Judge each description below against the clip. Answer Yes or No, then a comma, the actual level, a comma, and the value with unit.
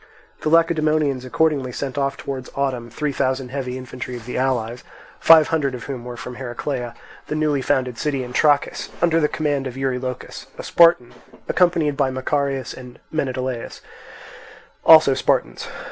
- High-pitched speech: No, low, 135 Hz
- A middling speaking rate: Yes, average, 155 wpm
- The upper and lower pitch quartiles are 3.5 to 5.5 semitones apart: No, average, 2.9 semitones